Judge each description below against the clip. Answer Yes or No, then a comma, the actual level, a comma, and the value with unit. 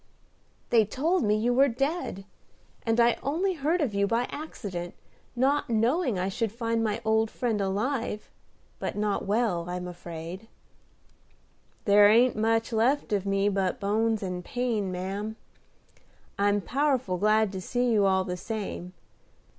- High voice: Yes, high, 220 Hz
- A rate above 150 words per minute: No, average, 145 wpm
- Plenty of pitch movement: No, average, 3.8 semitones